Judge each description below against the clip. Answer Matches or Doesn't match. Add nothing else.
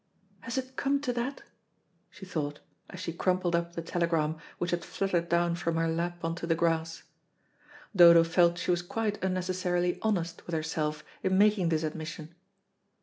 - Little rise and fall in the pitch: Matches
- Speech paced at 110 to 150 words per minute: Doesn't match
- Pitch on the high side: Doesn't match